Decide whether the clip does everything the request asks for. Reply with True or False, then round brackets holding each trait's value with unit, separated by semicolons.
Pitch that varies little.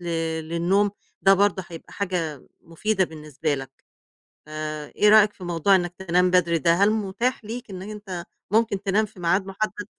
False (3.5 semitones)